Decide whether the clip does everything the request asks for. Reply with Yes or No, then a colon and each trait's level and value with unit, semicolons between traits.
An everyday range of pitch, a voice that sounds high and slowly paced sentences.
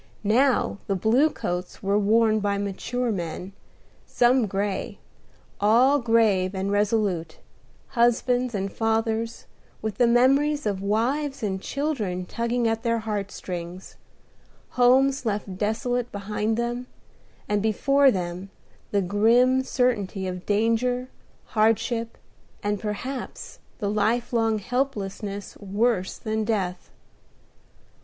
Yes: average, 3.4 semitones; high, 220 Hz; slow, 110 wpm